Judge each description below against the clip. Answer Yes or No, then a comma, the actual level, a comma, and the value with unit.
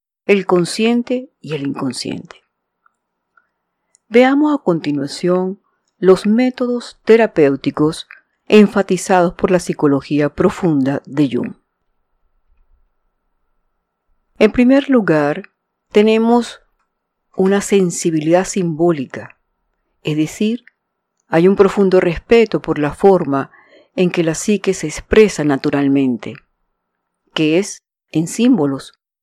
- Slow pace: Yes, slow, 90 wpm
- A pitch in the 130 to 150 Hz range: No, medium, 185 Hz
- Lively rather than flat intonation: Yes, wide, 5.9 semitones